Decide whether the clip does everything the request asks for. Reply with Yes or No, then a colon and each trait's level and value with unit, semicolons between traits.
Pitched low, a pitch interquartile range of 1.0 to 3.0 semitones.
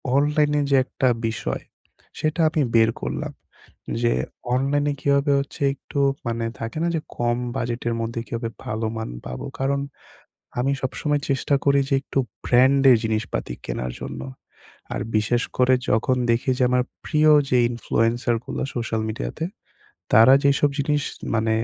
No: low, 125 Hz; average, 3.6 semitones